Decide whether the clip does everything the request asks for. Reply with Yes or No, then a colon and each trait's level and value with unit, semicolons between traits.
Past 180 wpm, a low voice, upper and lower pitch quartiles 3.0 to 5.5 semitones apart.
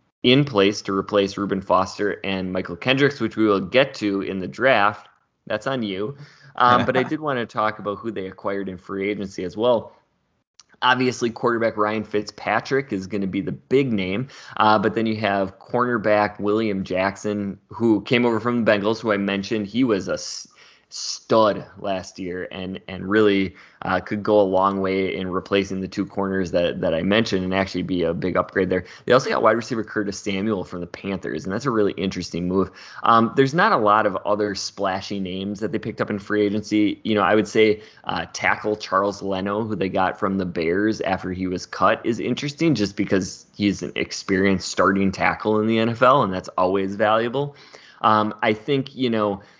No: average, 200 wpm; low, 105 Hz; narrow, 2.4 semitones